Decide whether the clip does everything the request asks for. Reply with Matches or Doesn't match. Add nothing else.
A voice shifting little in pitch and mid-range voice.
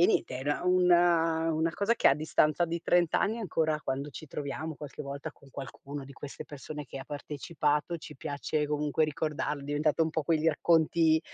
Matches